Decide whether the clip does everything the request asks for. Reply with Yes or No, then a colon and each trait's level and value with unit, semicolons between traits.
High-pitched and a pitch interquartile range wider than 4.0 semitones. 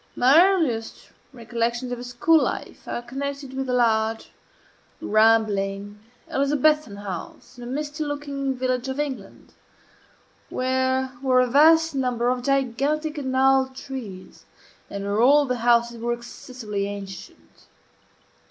No: very high, 255 Hz; average, 3.2 semitones